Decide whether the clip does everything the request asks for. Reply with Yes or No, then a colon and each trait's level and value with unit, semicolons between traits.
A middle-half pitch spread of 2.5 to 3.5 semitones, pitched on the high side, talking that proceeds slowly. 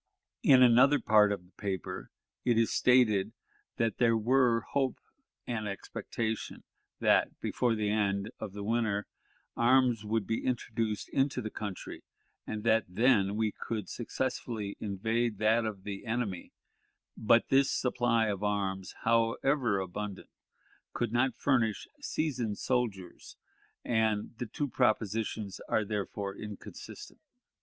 No: average, 2.8 semitones; low, 110 Hz; slow, 130 wpm